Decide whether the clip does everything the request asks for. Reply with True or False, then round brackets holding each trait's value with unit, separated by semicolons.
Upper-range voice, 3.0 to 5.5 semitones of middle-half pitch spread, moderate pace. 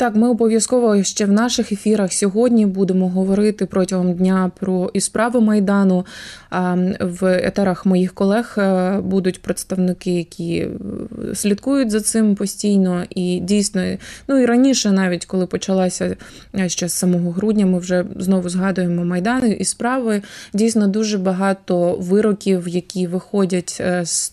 False (195 Hz; 2.5 semitones; 130 wpm)